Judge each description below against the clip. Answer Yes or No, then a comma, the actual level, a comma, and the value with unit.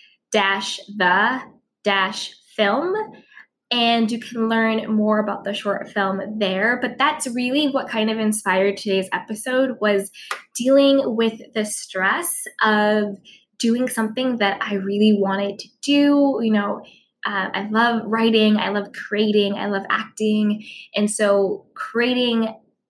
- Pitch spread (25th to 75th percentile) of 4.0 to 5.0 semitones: No, average, 3.1 semitones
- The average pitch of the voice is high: Yes, high, 220 Hz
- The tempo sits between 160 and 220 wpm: No, slow, 135 wpm